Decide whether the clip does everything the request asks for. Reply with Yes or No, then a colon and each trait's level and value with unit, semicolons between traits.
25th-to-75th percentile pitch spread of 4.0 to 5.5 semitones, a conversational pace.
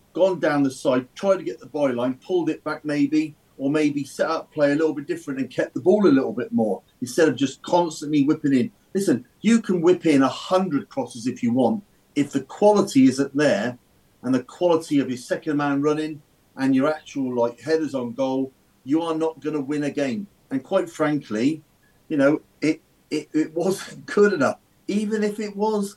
No: average, 5.2 semitones; fast, 210 wpm